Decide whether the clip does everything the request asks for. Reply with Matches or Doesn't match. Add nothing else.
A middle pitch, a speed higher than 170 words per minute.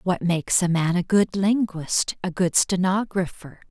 Doesn't match